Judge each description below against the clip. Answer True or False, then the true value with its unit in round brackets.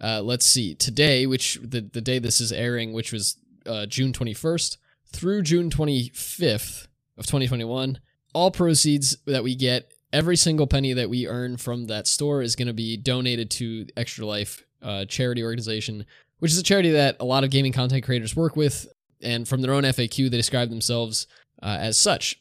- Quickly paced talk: False (185 wpm)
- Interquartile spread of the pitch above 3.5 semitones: False (3.2 semitones)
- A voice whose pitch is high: False (125 Hz)